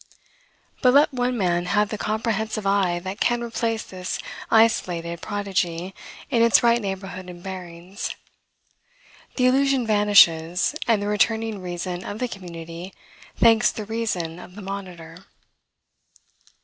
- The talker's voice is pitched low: No, high, 200 Hz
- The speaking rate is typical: No, slow, 130 wpm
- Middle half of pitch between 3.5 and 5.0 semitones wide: Yes, average, 4.1 semitones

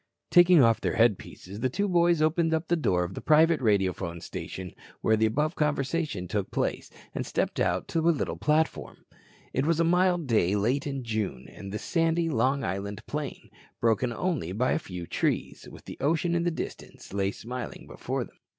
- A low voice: Yes, low, 130 Hz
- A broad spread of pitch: Yes, wide, 8.0 semitones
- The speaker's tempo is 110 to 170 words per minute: No, average, 185 wpm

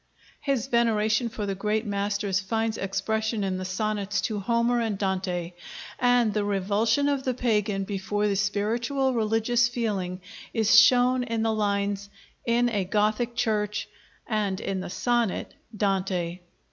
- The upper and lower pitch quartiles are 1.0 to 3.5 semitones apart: Yes, average, 2.9 semitones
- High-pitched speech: Yes, high, 215 Hz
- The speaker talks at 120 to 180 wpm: Yes, average, 145 wpm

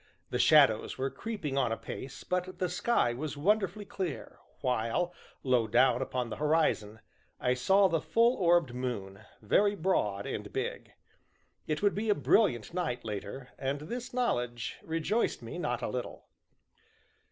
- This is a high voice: No, medium, 150 Hz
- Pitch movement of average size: No, wide, 7.8 semitones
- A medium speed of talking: Yes, average, 150 wpm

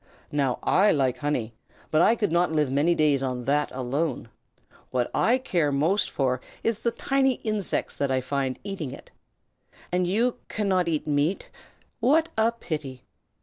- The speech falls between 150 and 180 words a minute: Yes, average, 160 wpm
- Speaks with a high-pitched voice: No, medium, 155 Hz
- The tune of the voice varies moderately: No, wide, 7.2 semitones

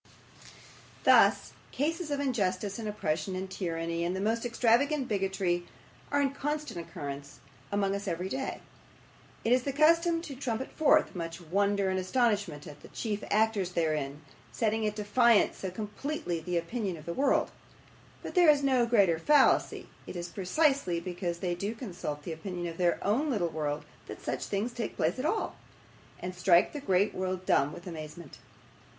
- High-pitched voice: Yes, high, 200 Hz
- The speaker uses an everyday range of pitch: No, wide, 6.2 semitones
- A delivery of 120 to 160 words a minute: No, average, 170 wpm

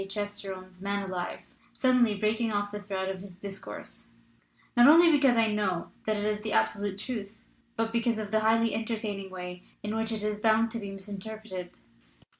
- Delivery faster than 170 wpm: Yes, average, 190 wpm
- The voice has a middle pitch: No, high, 210 Hz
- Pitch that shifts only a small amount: Yes, narrow, 2.3 semitones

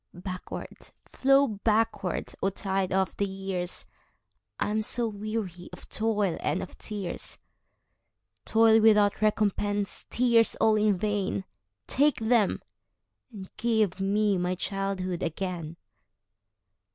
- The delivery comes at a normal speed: No, slow, 105 wpm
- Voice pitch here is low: No, high, 205 Hz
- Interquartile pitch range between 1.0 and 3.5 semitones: Yes, average, 2.8 semitones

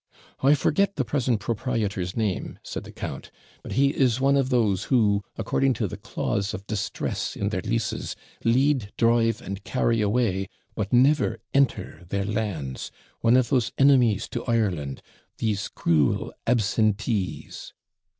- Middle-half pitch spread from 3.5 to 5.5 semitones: Yes, average, 4.1 semitones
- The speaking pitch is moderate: No, low, 110 Hz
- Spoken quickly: No, average, 145 wpm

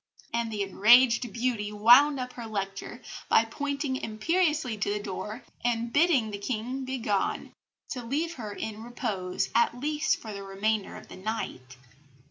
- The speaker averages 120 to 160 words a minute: Yes, average, 155 wpm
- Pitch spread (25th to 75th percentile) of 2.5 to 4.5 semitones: Yes, average, 3.8 semitones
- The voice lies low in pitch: No, high, 230 Hz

